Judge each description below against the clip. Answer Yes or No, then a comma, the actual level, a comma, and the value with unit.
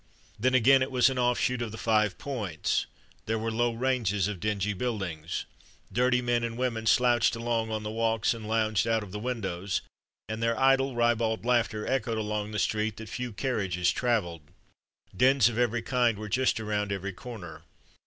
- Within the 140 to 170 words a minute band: No, average, 180 wpm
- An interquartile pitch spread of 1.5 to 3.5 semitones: Yes, narrow, 2.6 semitones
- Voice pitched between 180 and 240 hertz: No, low, 115 Hz